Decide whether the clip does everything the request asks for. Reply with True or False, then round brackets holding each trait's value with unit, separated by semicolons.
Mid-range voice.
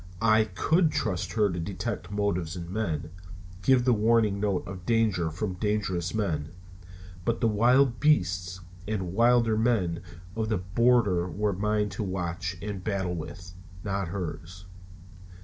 False (100 Hz)